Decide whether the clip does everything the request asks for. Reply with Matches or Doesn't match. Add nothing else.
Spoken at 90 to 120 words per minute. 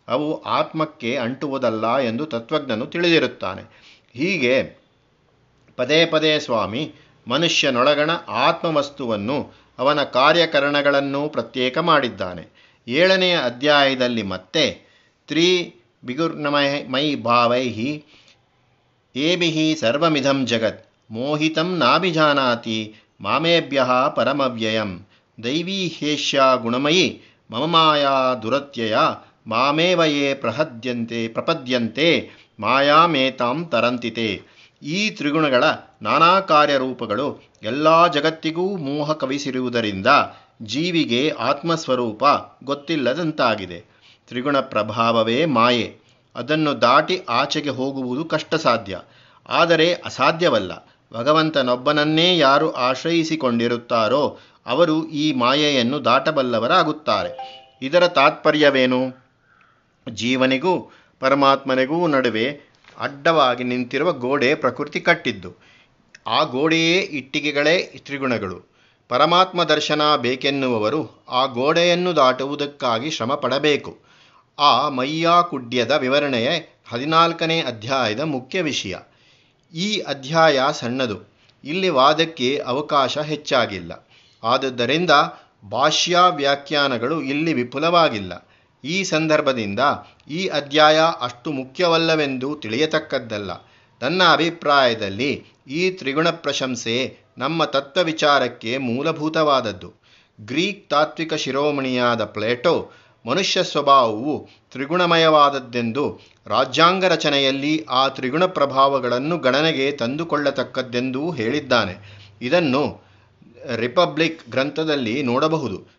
Doesn't match